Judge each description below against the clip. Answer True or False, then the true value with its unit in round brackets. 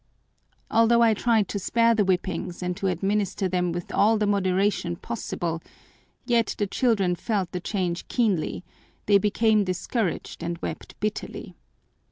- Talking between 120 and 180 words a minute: True (145 wpm)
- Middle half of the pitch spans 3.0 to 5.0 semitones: True (3.4 semitones)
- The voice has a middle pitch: False (200 Hz)